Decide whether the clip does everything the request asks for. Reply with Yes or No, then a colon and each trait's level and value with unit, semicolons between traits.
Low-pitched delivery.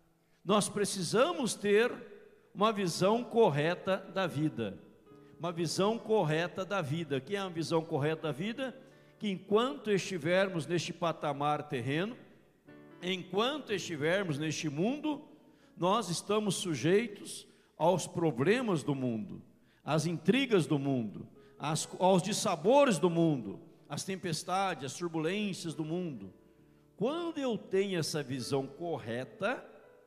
No: medium, 175 Hz